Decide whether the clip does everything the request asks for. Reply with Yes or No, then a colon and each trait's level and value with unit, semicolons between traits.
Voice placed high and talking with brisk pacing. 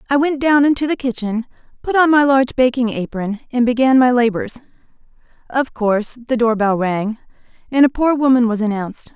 No: high, 245 Hz; average, 185 wpm